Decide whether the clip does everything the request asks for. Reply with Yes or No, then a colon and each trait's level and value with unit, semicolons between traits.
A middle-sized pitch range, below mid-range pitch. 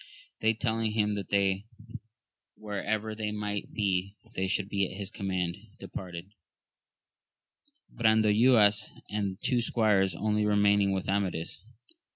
No: narrow, 2.0 semitones; low, 105 Hz